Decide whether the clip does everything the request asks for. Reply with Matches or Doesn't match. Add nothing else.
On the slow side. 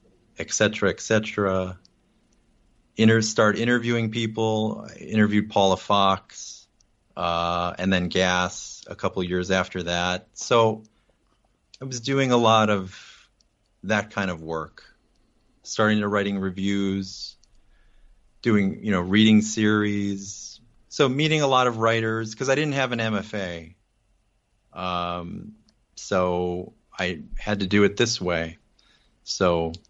Matches